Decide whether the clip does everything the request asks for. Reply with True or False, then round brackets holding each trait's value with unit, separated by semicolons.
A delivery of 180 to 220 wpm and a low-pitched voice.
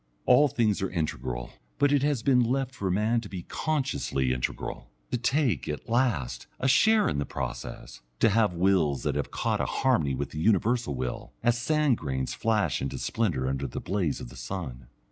True (190 wpm; 100 Hz)